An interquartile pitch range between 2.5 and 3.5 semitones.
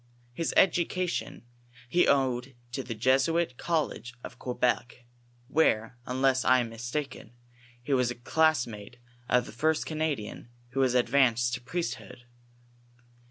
No: average, 4.1 semitones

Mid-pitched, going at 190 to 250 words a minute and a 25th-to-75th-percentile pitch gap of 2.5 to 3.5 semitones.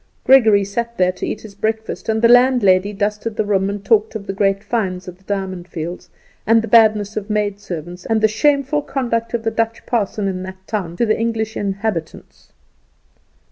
No: high, 210 Hz; average, 195 wpm; average, 2.8 semitones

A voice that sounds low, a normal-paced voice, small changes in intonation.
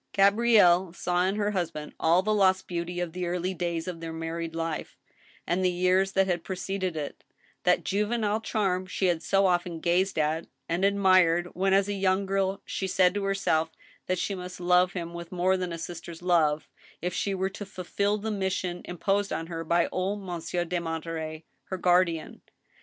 No: medium, 180 Hz; average, 195 wpm; narrow, 2.2 semitones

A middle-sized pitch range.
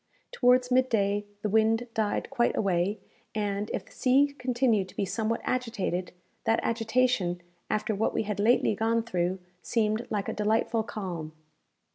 Yes: average, 3.1 semitones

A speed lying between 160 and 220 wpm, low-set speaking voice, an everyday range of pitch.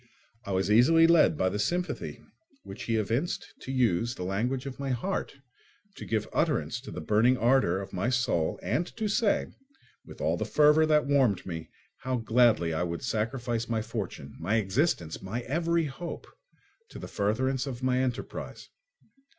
Yes: average, 170 wpm; low, 120 Hz; average, 5.0 semitones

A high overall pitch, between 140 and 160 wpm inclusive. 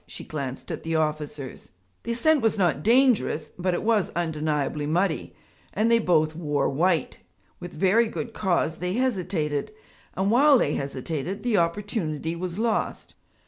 No: medium, 175 Hz; average, 150 wpm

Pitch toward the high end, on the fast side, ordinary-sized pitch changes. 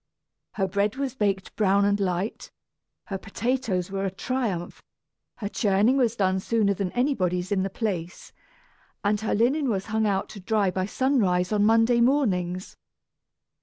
No: high, 205 Hz; average, 155 wpm; average, 3.3 semitones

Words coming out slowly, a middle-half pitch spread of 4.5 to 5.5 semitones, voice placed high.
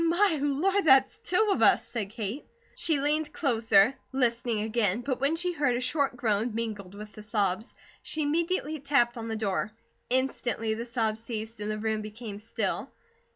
No: average, 175 wpm; average, 5.0 semitones; high, 240 Hz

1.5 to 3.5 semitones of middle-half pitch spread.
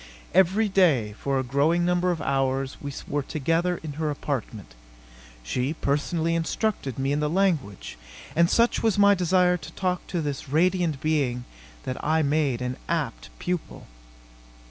No: average, 4.7 semitones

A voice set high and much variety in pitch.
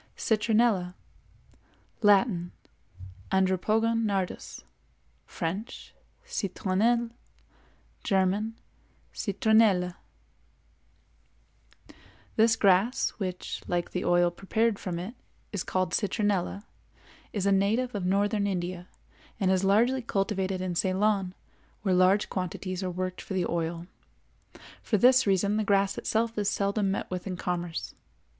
No: high, 195 Hz; average, 2.7 semitones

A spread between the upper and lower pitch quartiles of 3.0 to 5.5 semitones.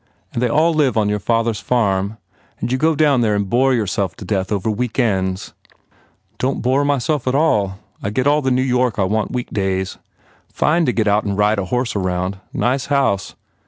Yes: average, 4.6 semitones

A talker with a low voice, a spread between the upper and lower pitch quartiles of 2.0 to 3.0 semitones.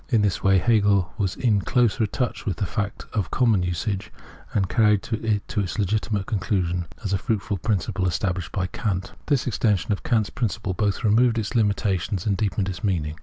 Yes: low, 100 Hz; average, 2.7 semitones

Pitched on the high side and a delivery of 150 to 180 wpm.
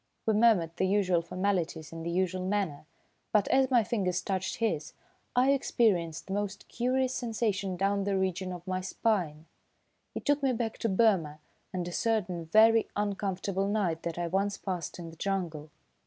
Yes: high, 195 Hz; average, 170 wpm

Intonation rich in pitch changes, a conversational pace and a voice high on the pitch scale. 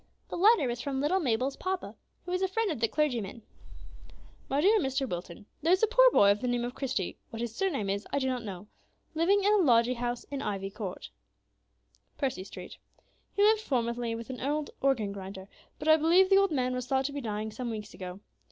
No: wide, 6.6 semitones; fast, 220 wpm; very high, 255 Hz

